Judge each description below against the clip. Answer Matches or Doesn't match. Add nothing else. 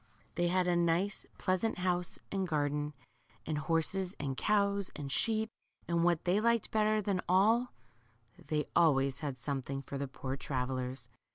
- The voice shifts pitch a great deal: Matches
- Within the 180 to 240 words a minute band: Doesn't match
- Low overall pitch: Doesn't match